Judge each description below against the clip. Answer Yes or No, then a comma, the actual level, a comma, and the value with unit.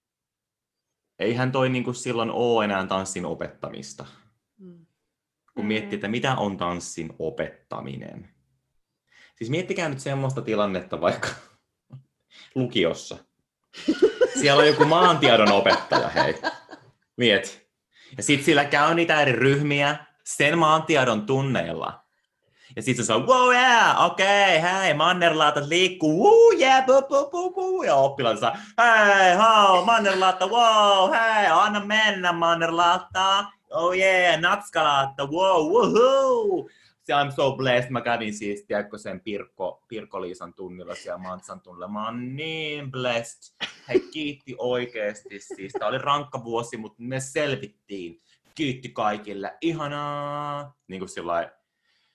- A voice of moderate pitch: Yes, medium, 145 Hz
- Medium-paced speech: Yes, average, 125 wpm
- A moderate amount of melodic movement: No, wide, 8.4 semitones